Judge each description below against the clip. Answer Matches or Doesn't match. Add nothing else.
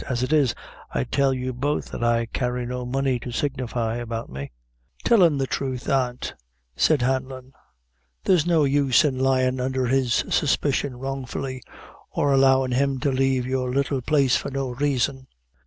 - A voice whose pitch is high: Doesn't match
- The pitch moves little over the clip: Matches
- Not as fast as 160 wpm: Doesn't match